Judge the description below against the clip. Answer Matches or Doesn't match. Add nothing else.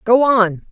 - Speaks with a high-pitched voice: Matches